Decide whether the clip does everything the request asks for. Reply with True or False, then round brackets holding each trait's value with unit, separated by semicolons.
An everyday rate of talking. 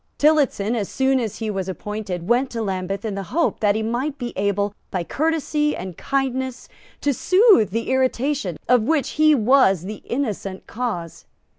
True (170 wpm)